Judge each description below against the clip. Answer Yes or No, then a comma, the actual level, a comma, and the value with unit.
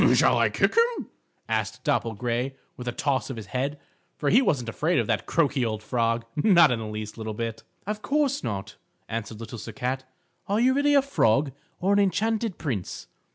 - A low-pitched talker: Yes, low, 130 Hz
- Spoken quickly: No, average, 195 wpm